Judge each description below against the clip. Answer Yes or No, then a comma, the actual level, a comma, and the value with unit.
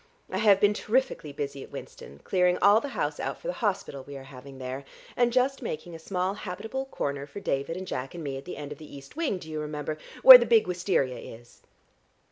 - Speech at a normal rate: No, fast, 230 wpm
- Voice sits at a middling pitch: Yes, medium, 175 Hz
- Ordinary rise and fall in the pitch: No, wide, 7.0 semitones